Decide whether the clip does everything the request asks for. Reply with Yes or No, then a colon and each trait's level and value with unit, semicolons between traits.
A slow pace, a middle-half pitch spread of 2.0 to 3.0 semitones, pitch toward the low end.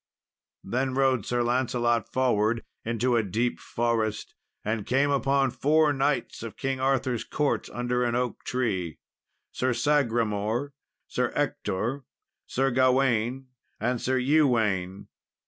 Yes: slow, 120 wpm; average, 2.7 semitones; low, 125 Hz